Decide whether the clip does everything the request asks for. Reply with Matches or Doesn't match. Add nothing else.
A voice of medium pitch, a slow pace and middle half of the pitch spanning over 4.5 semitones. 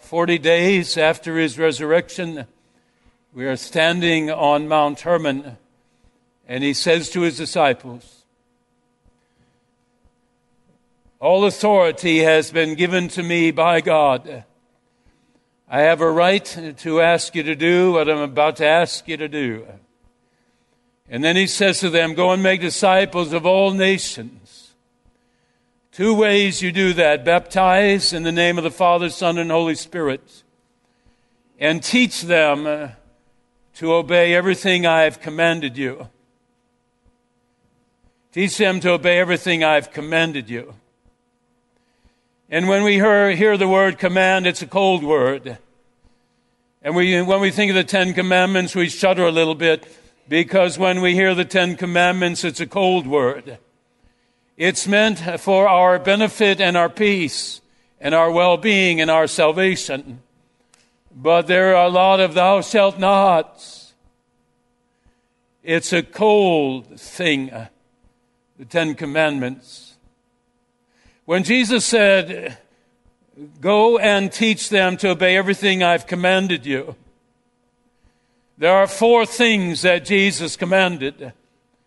Doesn't match